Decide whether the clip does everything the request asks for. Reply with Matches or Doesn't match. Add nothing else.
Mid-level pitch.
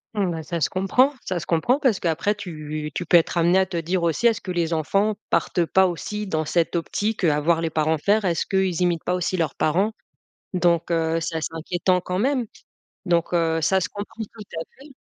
Matches